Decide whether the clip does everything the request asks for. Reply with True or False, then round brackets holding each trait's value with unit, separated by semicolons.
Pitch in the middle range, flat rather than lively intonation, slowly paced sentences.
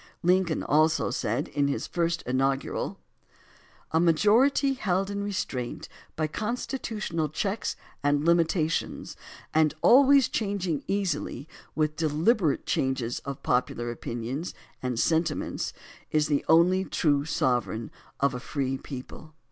False (155 Hz; 5.4 semitones; 115 wpm)